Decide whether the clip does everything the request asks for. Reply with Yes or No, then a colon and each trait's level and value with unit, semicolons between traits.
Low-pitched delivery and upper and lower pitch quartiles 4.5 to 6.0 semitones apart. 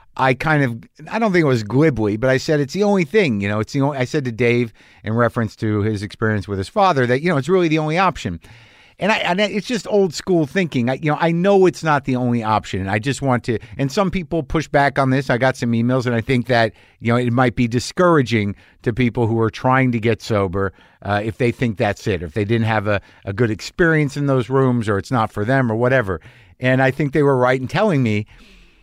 Yes: low, 125 Hz; average, 5.2 semitones